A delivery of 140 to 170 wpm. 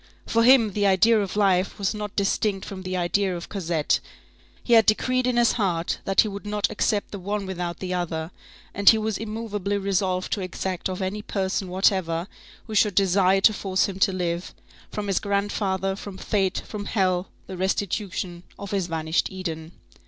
No: average, 180 wpm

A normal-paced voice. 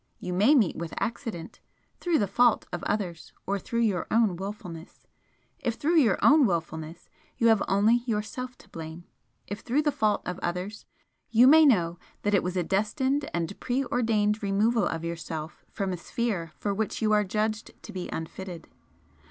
Yes: average, 175 wpm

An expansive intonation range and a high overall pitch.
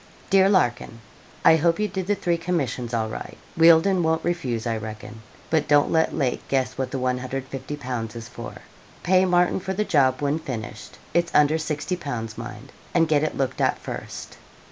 No: wide, 5.7 semitones; medium, 145 Hz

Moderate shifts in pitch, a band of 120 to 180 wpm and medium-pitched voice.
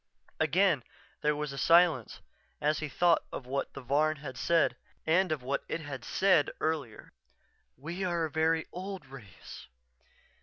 Yes: average, 3.5 semitones; average, 160 wpm; medium, 155 Hz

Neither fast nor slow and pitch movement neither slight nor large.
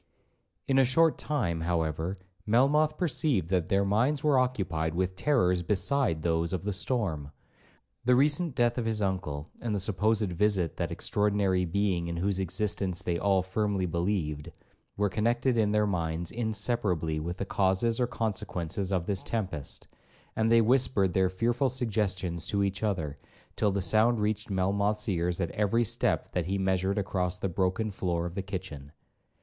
Yes: average, 165 wpm; average, 4.0 semitones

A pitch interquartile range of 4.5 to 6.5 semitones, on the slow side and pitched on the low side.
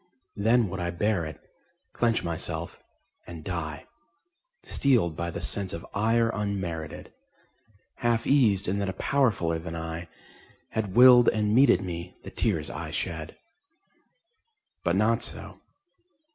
Yes: average, 5.1 semitones; slow, 130 wpm; very low, 95 Hz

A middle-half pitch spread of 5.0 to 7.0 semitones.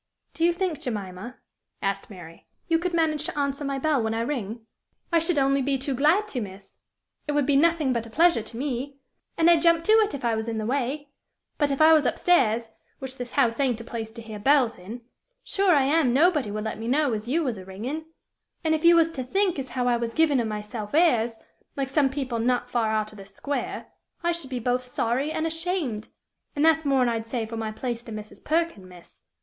Yes: wide, 5.5 semitones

